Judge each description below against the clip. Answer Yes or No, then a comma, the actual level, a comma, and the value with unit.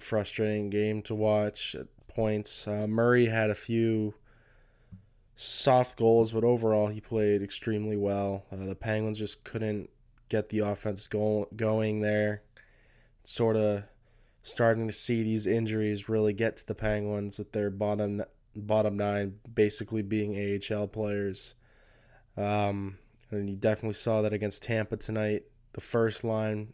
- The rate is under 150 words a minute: Yes, average, 140 wpm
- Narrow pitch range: Yes, narrow, 1.3 semitones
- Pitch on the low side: Yes, low, 105 Hz